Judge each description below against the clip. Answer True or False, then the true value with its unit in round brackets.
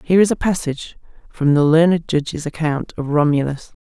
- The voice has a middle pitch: True (155 Hz)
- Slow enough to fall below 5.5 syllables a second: False (5.8 syllables/s)